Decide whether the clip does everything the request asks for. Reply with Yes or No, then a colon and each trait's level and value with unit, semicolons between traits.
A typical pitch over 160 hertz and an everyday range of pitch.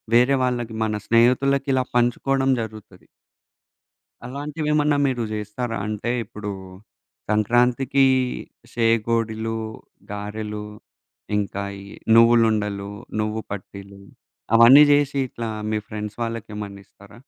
No: low, 115 Hz; average, 3.0 semitones